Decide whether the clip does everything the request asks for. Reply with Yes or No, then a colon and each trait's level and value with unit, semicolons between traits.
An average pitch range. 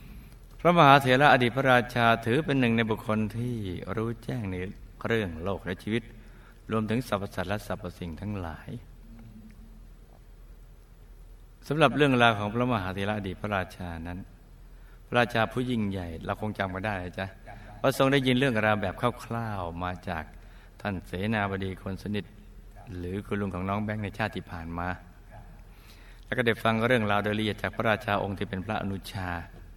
Yes: average, 3.5 semitones